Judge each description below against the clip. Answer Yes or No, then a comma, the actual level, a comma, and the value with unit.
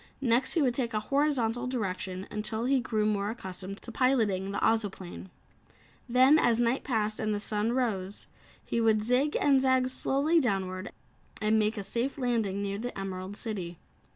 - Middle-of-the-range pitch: No, high, 220 Hz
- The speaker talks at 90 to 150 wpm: No, average, 170 wpm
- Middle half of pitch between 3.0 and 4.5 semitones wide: Yes, average, 4.0 semitones